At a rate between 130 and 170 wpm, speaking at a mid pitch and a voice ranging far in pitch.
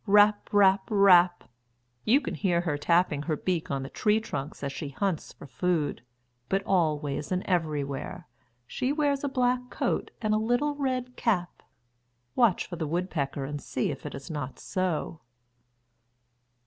Yes: average, 160 wpm; medium, 180 Hz; wide, 6.3 semitones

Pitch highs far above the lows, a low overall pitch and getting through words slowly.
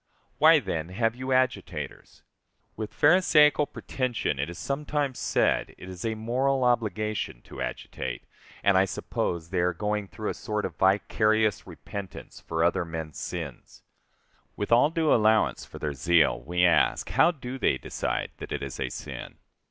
No: wide, 6.4 semitones; low, 105 Hz; average, 160 wpm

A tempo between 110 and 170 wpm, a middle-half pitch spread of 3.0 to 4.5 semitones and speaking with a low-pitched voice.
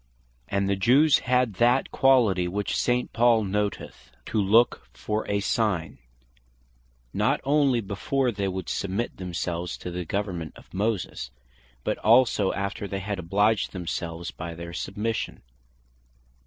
Yes: slow, 135 wpm; average, 4.0 semitones; low, 100 Hz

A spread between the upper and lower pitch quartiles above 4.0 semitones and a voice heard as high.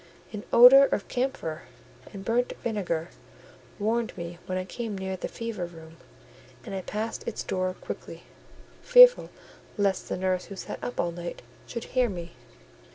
Yes: average, 4.6 semitones; high, 195 Hz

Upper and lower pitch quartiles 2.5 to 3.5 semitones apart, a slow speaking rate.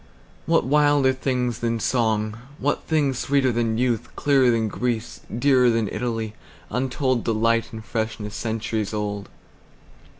Yes: average, 2.8 semitones; slow, 110 wpm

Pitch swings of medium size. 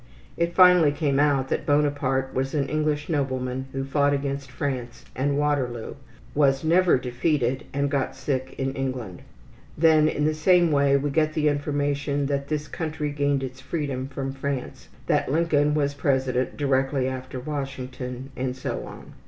No: narrow, 2.0 semitones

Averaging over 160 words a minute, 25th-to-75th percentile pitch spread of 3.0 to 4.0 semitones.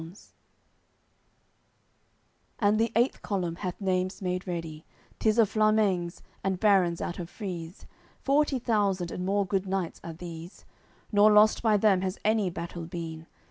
No: average, 145 wpm; average, 3.5 semitones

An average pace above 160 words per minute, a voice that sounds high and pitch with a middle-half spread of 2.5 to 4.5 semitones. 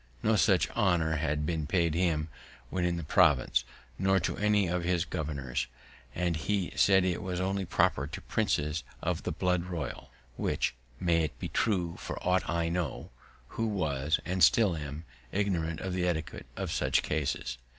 No: average, 170 wpm; very low, 85 Hz; average, 3.0 semitones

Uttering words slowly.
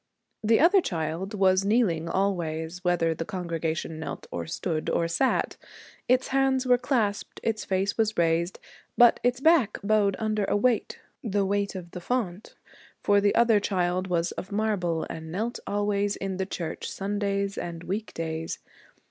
No: average, 160 wpm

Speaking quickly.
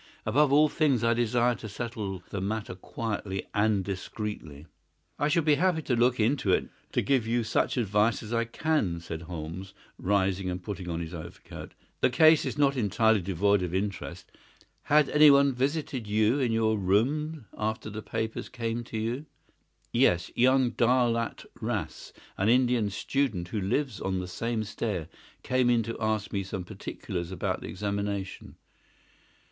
No: average, 165 wpm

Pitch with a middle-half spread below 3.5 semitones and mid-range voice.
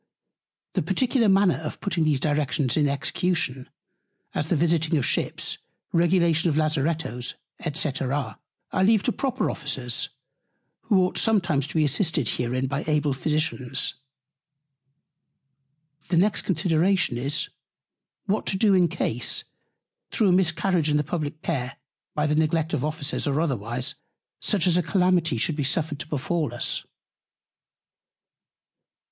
No: average, 3.9 semitones; medium, 155 Hz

